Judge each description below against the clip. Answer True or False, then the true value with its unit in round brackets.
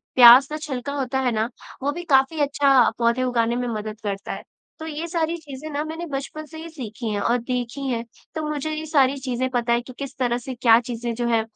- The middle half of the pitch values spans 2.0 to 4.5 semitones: True (3.7 semitones)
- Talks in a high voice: True (260 Hz)